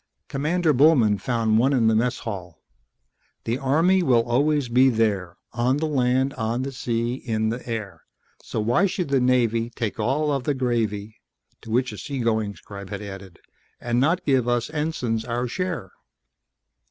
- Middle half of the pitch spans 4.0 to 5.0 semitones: No, average, 3.6 semitones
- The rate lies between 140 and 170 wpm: Yes, average, 165 wpm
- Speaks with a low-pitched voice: Yes, low, 120 Hz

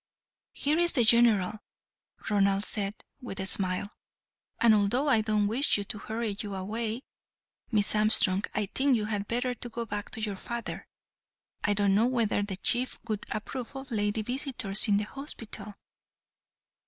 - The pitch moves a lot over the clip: No, average, 2.8 semitones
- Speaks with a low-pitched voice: No, high, 215 Hz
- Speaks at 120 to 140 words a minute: No, average, 155 wpm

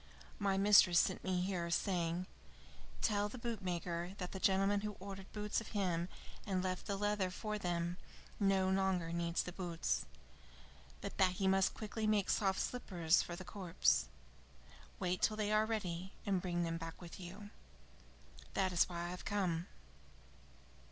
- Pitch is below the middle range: No, medium, 185 Hz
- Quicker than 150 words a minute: Yes, average, 160 wpm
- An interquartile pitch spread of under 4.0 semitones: Yes, average, 2.7 semitones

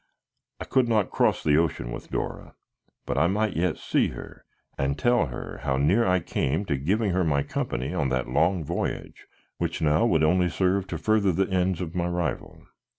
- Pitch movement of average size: Yes, average, 4.4 semitones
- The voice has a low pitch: Yes, very low, 85 Hz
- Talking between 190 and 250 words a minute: Yes, average, 195 wpm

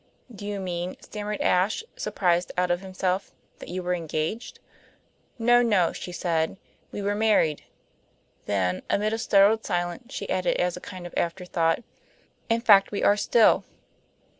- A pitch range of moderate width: Yes, average, 3.1 semitones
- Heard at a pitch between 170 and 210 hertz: Yes, medium, 185 Hz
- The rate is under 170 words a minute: Yes, average, 155 wpm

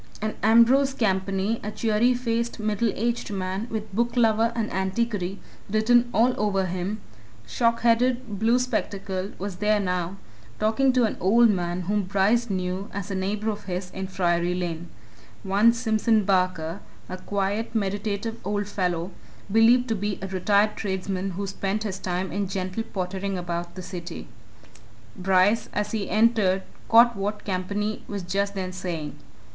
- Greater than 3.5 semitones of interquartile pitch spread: No, average, 3.0 semitones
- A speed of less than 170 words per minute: Yes, average, 150 wpm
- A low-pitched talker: No, high, 200 Hz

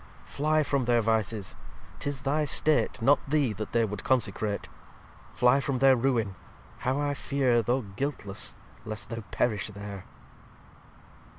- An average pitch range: Yes, average, 4.4 semitones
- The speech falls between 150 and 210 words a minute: No, slow, 135 wpm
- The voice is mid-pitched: No, low, 120 Hz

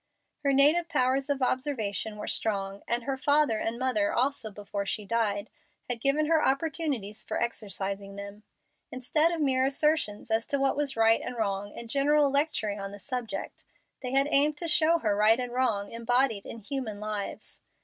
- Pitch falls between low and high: No, very high, 250 Hz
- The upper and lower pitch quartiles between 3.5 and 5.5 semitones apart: Yes, average, 5.1 semitones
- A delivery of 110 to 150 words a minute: No, average, 180 wpm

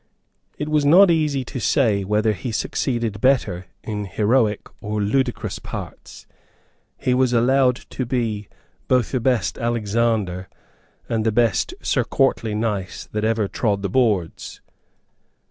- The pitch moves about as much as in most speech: Yes, average, 3.5 semitones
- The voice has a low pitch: Yes, low, 115 Hz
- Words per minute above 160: No, average, 140 wpm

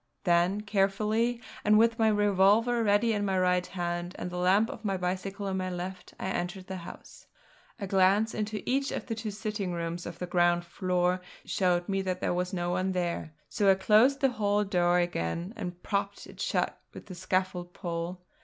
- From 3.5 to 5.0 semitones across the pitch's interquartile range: No, average, 2.8 semitones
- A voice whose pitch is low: No, high, 190 Hz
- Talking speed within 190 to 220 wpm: Yes, average, 195 wpm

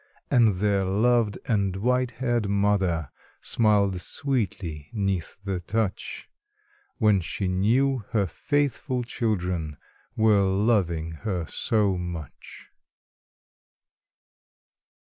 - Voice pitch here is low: Yes, low, 100 Hz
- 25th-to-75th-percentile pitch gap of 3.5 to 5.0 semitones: Yes, average, 4.0 semitones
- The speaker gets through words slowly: Yes, slow, 90 wpm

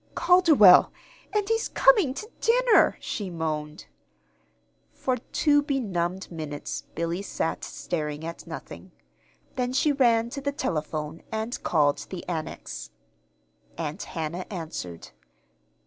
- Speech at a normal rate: No, slow, 115 wpm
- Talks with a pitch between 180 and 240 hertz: Yes, medium, 185 Hz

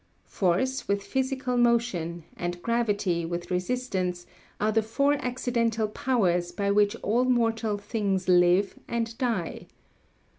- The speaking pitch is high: Yes, high, 215 Hz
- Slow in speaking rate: Yes, slow, 120 wpm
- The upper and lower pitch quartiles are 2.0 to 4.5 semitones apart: No, average, 4.9 semitones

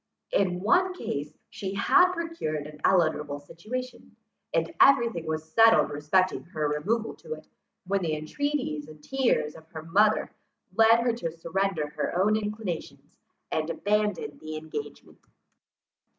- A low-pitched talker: No, medium, 185 Hz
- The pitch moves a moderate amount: No, wide, 6.4 semitones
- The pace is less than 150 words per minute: Yes, average, 140 wpm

